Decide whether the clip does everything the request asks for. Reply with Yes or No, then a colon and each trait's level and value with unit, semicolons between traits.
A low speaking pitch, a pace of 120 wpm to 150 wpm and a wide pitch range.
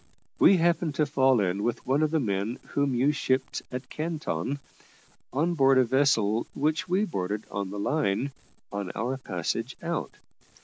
No: low, 130 Hz; average, 165 wpm; wide, 6.3 semitones